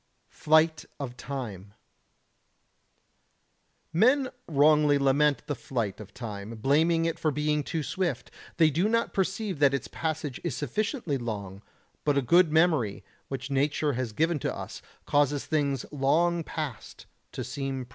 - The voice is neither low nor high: Yes, medium, 145 Hz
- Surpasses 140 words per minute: Yes, average, 150 wpm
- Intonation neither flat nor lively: Yes, average, 3.8 semitones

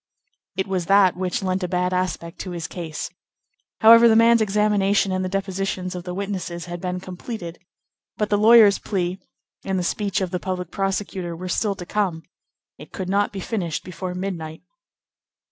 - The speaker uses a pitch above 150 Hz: Yes, medium, 185 Hz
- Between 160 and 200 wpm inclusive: Yes, average, 180 wpm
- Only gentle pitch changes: Yes, narrow, 2.0 semitones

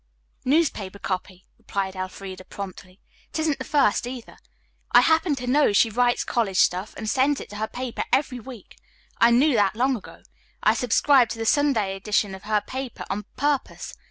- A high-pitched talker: Yes, high, 230 Hz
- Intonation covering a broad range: No, average, 4.9 semitones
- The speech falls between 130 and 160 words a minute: No, average, 180 wpm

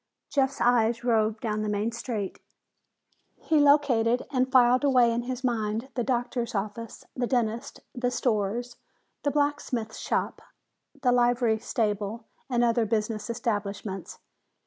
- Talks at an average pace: No, slow, 130 wpm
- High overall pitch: Yes, high, 235 Hz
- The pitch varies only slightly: Yes, narrow, 2.3 semitones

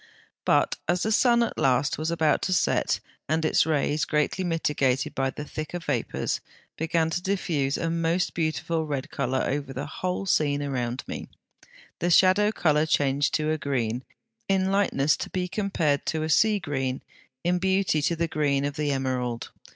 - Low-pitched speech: No, medium, 155 Hz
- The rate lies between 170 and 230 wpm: Yes, average, 175 wpm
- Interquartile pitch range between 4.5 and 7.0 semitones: No, average, 4.0 semitones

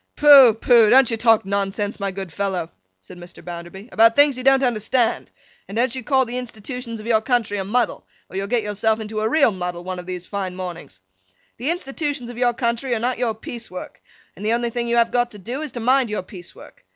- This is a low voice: No, high, 225 Hz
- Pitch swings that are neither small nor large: Yes, average, 3.9 semitones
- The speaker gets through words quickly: Yes, fast, 235 wpm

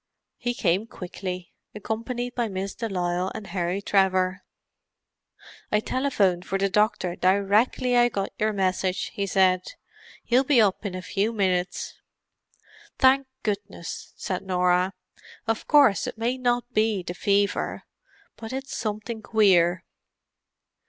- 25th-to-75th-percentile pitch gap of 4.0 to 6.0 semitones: No, average, 3.6 semitones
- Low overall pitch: No, high, 200 Hz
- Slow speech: Yes, slow, 130 wpm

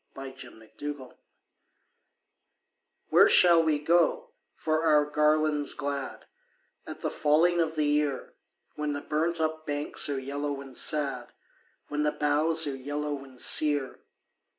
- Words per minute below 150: Yes, average, 140 wpm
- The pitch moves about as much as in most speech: No, narrow, 1.7 semitones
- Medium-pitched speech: Yes, medium, 150 Hz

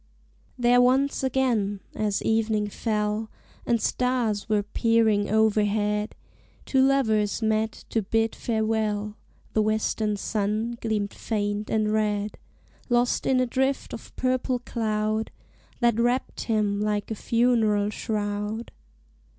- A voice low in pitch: No, high, 220 Hz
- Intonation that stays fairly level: Yes, narrow, 2.1 semitones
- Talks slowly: Yes, slow, 120 wpm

